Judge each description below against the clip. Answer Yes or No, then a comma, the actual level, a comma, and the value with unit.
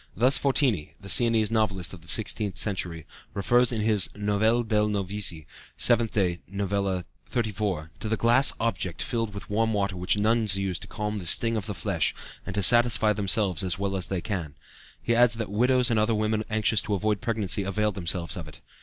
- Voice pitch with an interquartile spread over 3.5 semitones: No, average, 2.8 semitones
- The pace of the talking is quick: No, average, 195 wpm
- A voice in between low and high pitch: No, low, 105 Hz